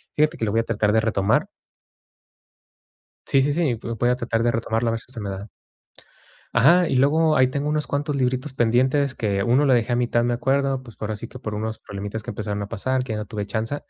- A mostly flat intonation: No, average, 3.5 semitones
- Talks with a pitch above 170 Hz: No, low, 120 Hz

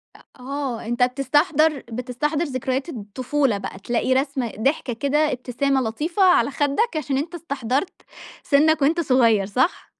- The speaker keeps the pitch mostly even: No, average, 3.4 semitones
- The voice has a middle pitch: No, very high, 275 Hz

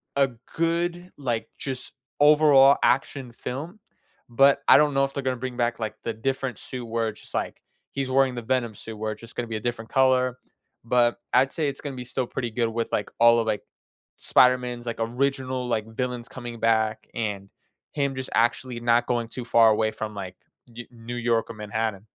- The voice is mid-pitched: No, low, 120 Hz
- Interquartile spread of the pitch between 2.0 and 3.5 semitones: Yes, average, 2.7 semitones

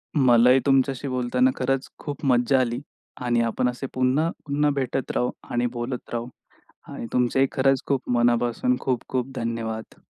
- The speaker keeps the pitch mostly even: Yes, narrow, 2.0 semitones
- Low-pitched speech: Yes, low, 125 Hz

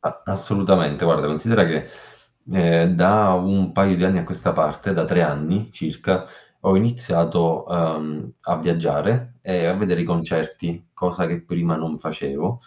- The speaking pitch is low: Yes, very low, 85 Hz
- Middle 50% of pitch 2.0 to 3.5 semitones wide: Yes, average, 2.7 semitones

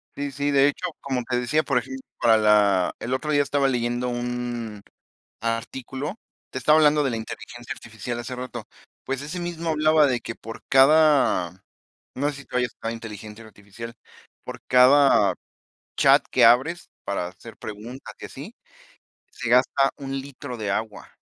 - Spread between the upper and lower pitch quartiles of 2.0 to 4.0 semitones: Yes, average, 3.7 semitones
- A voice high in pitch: No, low, 125 Hz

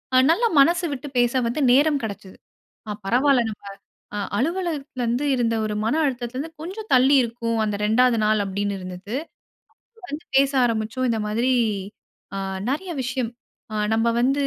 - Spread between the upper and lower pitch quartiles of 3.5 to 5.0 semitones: Yes, average, 4.0 semitones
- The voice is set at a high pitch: Yes, high, 245 Hz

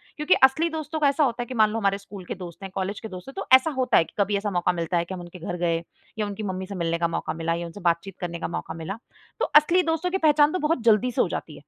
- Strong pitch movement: Yes, wide, 8.0 semitones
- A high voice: Yes, high, 200 Hz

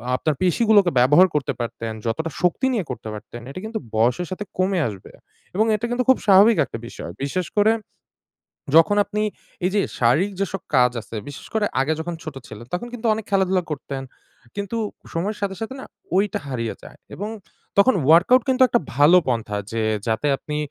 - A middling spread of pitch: No, wide, 7.6 semitones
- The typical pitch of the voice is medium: Yes, medium, 180 Hz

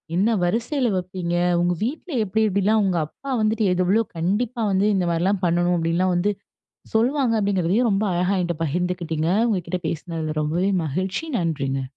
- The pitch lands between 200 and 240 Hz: No, medium, 185 Hz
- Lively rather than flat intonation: No, average, 3.9 semitones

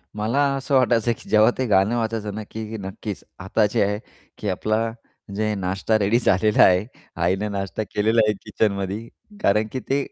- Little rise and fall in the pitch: Yes, narrow, 2.3 semitones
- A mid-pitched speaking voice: No, low, 105 Hz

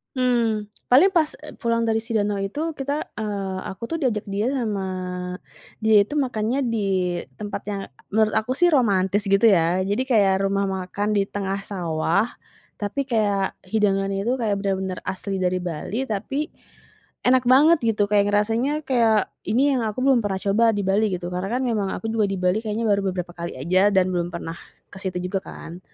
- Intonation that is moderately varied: Yes, average, 3.3 semitones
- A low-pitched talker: No, high, 205 Hz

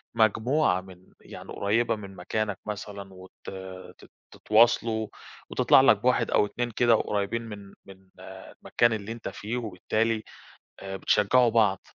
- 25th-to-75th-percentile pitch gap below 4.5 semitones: Yes, average, 2.7 semitones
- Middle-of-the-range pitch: No, low, 110 Hz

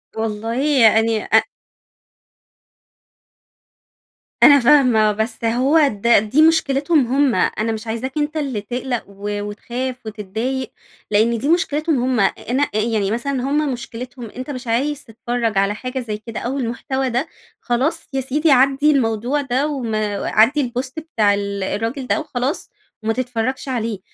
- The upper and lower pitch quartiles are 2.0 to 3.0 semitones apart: No, average, 3.6 semitones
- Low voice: No, high, 245 Hz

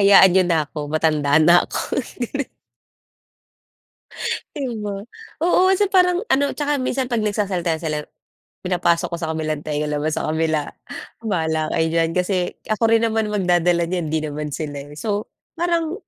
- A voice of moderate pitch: Yes, medium, 175 Hz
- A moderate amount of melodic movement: No, wide, 5.8 semitones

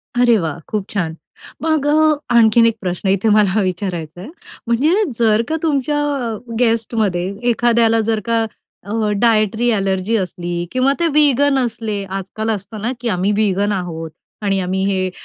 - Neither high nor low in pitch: No, high, 215 Hz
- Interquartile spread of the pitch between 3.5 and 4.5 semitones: Yes, average, 3.8 semitones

